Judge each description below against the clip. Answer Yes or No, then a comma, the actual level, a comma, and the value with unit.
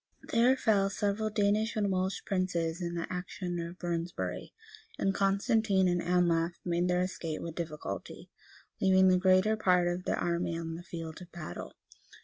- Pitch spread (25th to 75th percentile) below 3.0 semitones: Yes, narrow, 2.4 semitones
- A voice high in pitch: No, medium, 180 Hz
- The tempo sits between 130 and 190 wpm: Yes, average, 165 wpm